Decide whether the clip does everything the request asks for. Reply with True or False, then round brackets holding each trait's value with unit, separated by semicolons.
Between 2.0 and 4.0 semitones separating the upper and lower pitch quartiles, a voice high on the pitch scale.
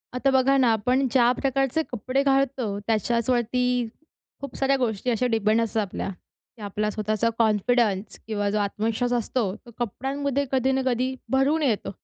True (3.5 semitones; 245 Hz)